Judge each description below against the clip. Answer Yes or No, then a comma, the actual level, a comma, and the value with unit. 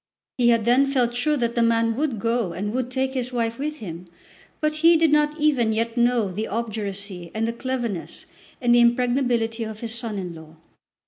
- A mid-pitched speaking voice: No, high, 235 Hz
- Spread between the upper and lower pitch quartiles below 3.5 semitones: Yes, average, 2.8 semitones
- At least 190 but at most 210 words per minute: Yes, average, 200 wpm